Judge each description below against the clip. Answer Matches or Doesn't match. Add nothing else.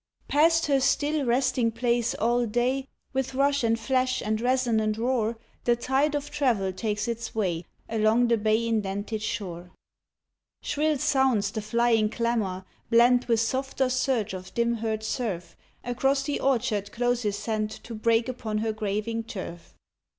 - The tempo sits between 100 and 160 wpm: Matches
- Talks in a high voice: Matches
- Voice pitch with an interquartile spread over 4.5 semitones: Doesn't match